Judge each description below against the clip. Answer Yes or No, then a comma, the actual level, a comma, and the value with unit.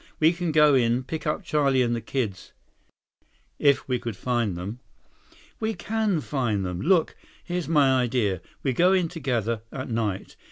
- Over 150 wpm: Yes, average, 165 wpm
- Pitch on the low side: Yes, low, 130 Hz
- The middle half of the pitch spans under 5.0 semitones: No, average, 5.3 semitones